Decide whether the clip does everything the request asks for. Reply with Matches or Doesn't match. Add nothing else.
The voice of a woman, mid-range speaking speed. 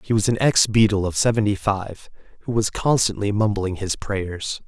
Doesn't match